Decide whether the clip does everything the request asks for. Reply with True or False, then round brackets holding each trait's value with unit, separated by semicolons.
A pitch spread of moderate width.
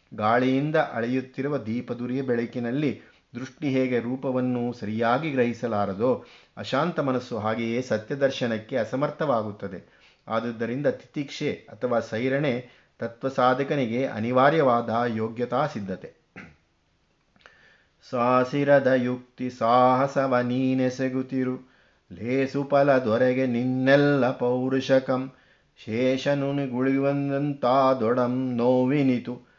False (1.9 semitones)